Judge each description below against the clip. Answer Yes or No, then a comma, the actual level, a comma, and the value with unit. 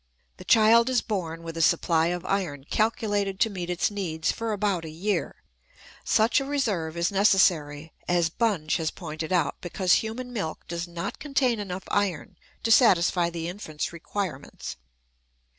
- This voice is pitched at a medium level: Yes, medium, 180 Hz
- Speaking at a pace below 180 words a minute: Yes, average, 160 wpm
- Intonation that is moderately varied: Yes, average, 4.3 semitones